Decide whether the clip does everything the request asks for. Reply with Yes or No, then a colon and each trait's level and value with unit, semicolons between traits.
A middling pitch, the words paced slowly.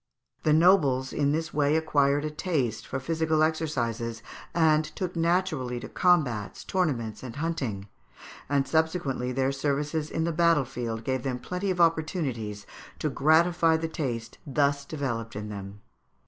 No: medium, 145 Hz; average, 145 wpm